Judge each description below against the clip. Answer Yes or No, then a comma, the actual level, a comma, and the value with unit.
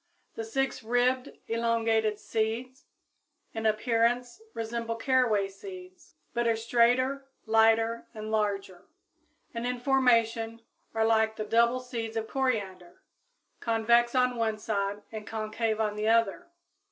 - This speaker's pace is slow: Yes, slow, 125 wpm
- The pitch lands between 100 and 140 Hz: No, high, 230 Hz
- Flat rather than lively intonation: Yes, narrow, 1.9 semitones